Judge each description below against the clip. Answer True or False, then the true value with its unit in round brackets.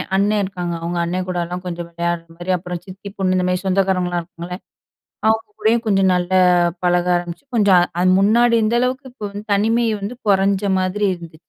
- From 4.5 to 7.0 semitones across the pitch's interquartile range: False (2.8 semitones)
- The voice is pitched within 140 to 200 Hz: True (185 Hz)